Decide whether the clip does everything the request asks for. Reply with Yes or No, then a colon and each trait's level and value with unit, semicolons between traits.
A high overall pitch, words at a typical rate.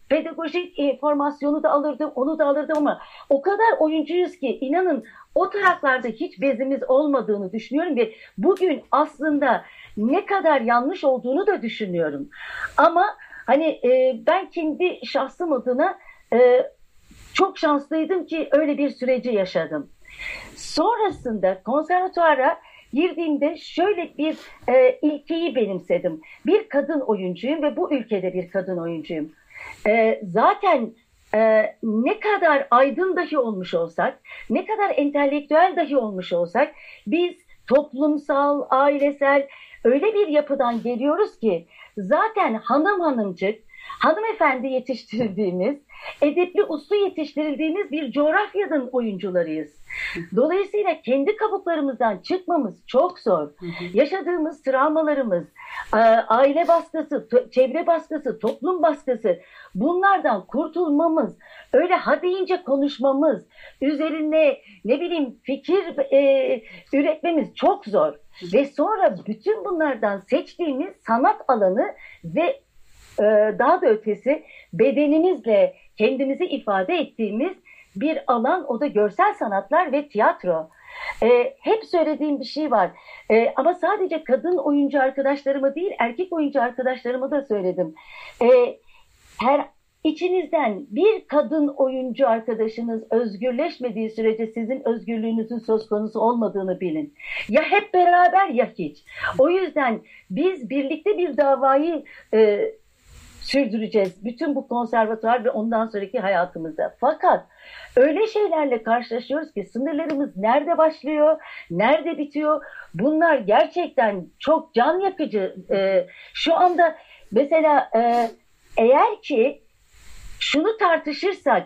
Yes: very high, 285 Hz; average, 110 wpm